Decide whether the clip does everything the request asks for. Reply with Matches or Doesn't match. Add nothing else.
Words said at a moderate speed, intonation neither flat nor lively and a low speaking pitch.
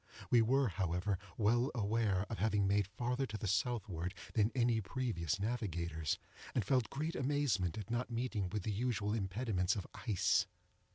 Matches